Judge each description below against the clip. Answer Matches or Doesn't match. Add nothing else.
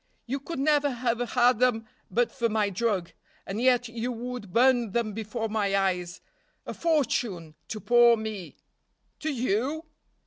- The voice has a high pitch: Matches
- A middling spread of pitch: Matches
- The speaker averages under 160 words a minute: Matches